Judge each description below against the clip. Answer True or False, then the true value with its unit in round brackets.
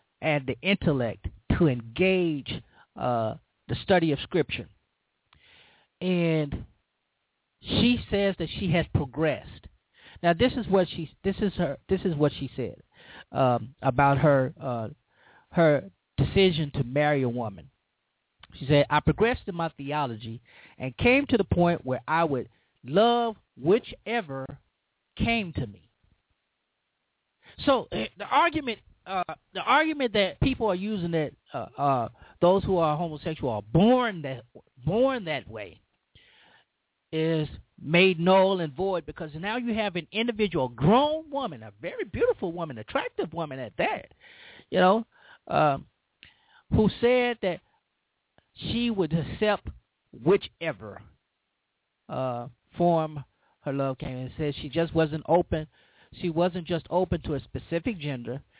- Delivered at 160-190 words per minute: False (135 wpm)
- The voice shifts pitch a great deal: True (6.4 semitones)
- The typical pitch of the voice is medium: True (165 Hz)